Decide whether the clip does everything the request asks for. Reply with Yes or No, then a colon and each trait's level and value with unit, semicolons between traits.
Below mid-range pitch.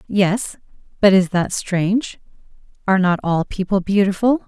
No: high, 195 Hz